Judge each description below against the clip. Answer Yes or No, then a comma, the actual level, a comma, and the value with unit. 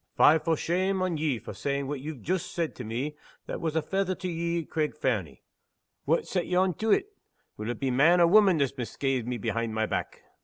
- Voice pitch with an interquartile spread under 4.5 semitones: No, wide, 5.5 semitones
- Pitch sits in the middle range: Yes, medium, 155 Hz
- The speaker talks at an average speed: No, fast, 230 wpm